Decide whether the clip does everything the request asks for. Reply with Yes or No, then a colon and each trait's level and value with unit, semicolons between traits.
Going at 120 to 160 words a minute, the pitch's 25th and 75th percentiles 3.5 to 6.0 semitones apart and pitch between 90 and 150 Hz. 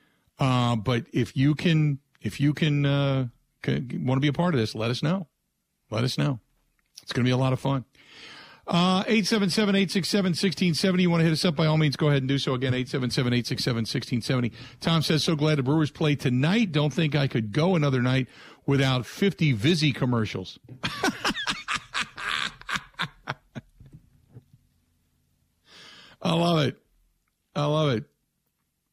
No: average, 180 wpm; average, 4.6 semitones; medium, 140 Hz